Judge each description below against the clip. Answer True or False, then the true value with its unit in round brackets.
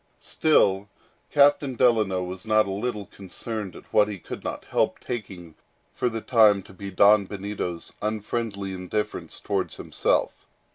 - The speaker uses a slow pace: False (145 wpm)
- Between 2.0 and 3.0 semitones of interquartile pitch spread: True (2.6 semitones)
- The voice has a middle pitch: False (105 Hz)